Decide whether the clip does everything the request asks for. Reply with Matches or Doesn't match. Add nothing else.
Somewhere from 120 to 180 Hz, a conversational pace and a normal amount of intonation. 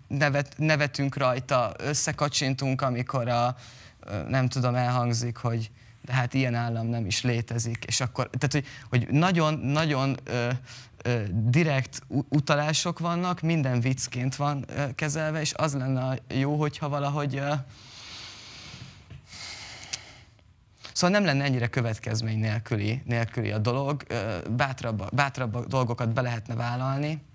Matches